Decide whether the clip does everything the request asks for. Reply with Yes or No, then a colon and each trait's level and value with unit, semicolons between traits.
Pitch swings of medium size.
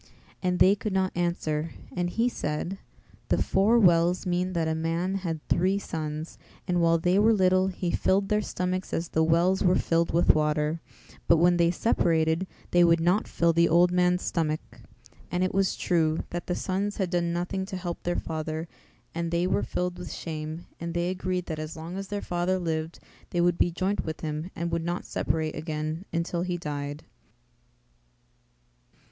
No: narrow, 2.2 semitones